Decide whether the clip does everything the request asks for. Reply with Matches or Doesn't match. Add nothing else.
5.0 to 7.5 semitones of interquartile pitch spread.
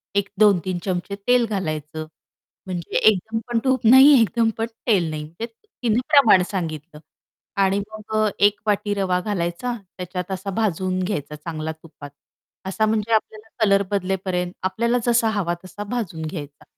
Doesn't match